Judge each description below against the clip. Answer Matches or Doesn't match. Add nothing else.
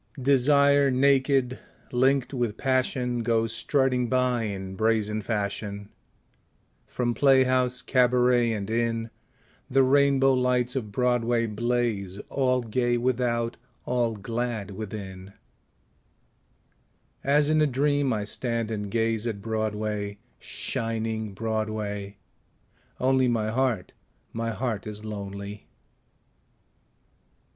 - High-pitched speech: Doesn't match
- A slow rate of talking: Matches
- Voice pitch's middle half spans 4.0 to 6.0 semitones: Doesn't match